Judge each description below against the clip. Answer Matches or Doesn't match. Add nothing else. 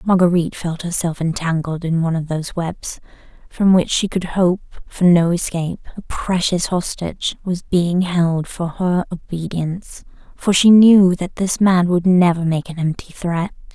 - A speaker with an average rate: Matches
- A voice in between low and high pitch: Matches